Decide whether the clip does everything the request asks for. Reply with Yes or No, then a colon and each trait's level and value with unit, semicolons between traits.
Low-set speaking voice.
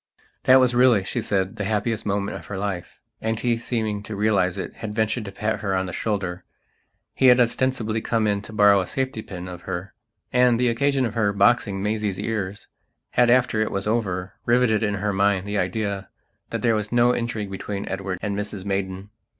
Yes: low, 105 Hz